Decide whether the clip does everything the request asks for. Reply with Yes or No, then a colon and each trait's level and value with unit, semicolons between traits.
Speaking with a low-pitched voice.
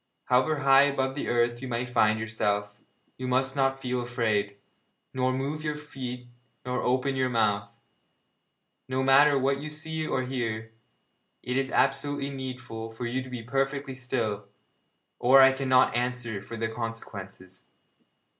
Yes: low, 125 Hz